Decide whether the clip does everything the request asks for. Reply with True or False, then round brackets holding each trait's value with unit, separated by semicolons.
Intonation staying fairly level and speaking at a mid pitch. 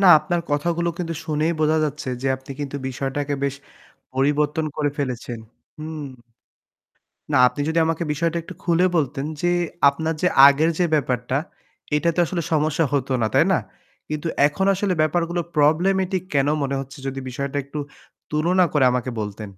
False (3.3 semitones; 150 Hz)